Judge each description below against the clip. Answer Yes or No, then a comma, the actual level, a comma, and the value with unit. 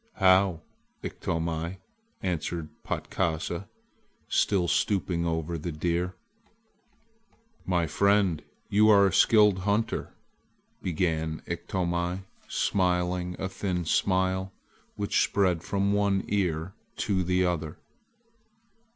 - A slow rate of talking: Yes, slow, 95 wpm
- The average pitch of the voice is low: Yes, very low, 90 Hz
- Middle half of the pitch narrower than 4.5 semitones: Yes, narrow, 2.4 semitones